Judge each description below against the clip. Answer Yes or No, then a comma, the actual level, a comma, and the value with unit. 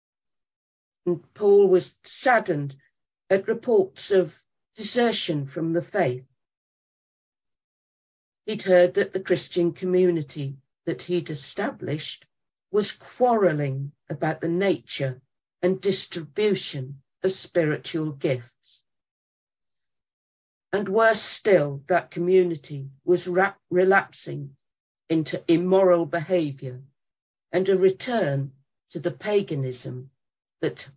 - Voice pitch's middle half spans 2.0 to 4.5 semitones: No, wide, 5.5 semitones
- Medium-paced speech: No, slow, 95 wpm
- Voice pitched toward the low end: No, medium, 170 Hz